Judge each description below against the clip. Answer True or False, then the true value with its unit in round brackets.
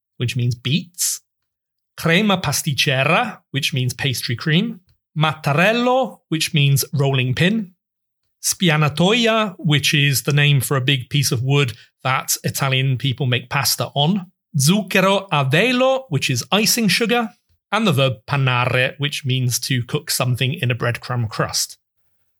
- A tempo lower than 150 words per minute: True (135 wpm)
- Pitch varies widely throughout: True (5.9 semitones)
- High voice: False (145 Hz)